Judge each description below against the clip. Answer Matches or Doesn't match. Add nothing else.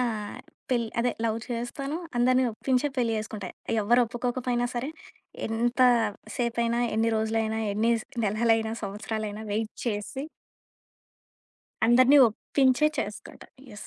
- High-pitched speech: Matches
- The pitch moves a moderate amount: Doesn't match